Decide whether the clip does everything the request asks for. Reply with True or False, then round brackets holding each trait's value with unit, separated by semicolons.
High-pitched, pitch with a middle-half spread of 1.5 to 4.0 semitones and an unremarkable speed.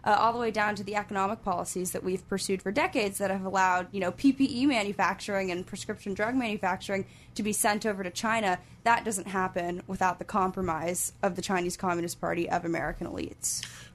True (195 Hz; 2.5 semitones; 195 wpm)